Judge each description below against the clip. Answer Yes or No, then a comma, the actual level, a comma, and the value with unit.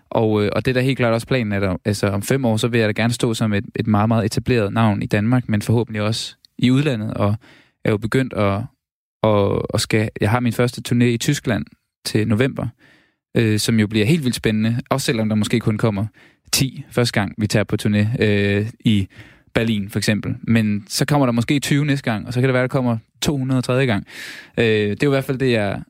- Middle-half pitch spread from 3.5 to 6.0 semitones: No, average, 3.1 semitones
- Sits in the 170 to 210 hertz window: No, low, 115 Hz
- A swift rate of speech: Yes, fast, 240 wpm